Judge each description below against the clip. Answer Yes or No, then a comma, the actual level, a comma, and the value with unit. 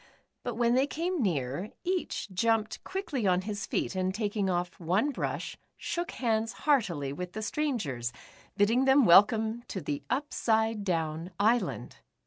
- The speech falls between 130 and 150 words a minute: Yes, average, 145 wpm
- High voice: Yes, high, 215 Hz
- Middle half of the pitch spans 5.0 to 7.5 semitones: Yes, average, 5.3 semitones